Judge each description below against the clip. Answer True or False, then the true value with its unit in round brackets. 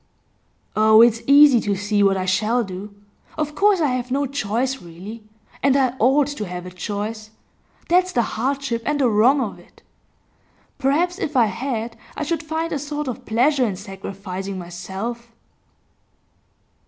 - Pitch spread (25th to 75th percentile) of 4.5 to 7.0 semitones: True (5.5 semitones)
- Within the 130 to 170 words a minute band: True (160 wpm)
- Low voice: False (235 Hz)